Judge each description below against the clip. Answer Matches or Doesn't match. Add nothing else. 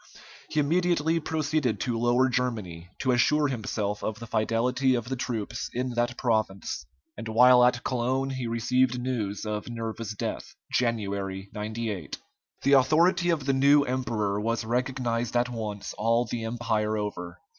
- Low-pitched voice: Matches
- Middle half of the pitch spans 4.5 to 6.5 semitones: Doesn't match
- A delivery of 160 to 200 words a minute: Doesn't match